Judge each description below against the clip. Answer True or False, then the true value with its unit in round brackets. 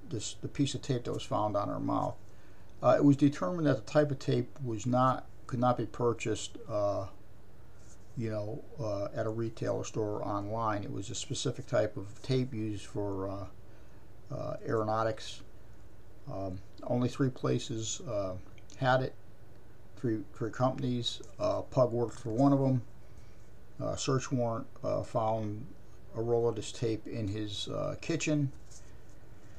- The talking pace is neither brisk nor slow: True (160 wpm)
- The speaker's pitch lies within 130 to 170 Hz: False (115 Hz)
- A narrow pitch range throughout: False (3.3 semitones)